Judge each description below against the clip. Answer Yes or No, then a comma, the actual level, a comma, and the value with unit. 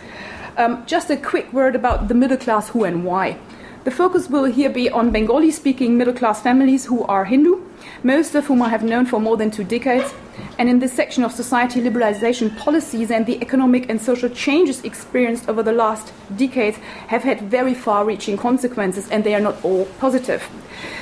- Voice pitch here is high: Yes, high, 245 Hz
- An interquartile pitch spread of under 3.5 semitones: Yes, average, 3.0 semitones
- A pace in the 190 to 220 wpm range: Yes, average, 195 wpm